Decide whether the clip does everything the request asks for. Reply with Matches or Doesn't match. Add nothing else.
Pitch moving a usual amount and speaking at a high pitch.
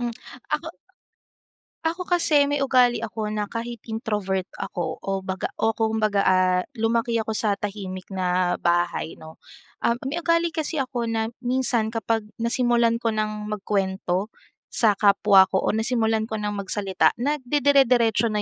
Matches